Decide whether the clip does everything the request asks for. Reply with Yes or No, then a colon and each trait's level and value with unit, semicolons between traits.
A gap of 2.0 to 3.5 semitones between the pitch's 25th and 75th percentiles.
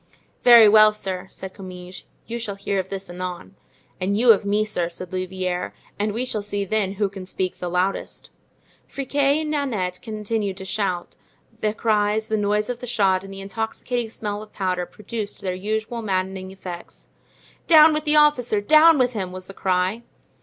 Yes: average, 3.1 semitones